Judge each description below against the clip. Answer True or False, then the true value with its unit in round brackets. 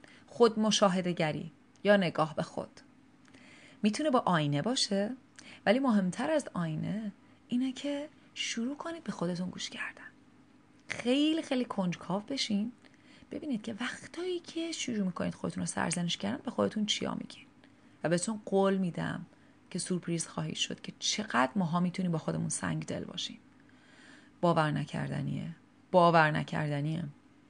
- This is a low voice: False (230 Hz)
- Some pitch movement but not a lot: False (7.0 semitones)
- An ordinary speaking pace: True (135 wpm)